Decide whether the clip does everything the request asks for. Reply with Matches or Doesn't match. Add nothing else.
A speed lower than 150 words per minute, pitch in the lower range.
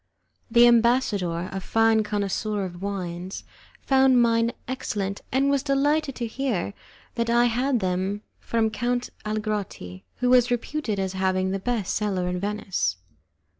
Doesn't match